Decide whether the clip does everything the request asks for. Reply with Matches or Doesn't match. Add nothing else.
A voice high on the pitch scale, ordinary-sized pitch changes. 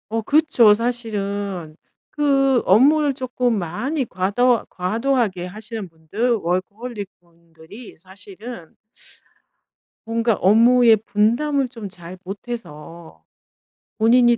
Matches